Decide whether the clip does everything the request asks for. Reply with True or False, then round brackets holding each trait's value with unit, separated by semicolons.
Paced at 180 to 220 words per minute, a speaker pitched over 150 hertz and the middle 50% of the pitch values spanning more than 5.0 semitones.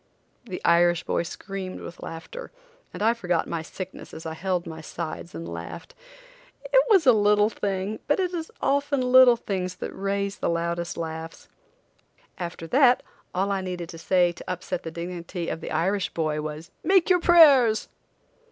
False (170 wpm; 185 Hz; 5.6 semitones)